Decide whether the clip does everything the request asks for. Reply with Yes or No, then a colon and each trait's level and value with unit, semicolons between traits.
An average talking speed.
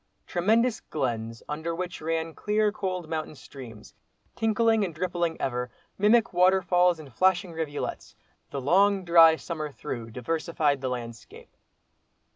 No: slow, 125 wpm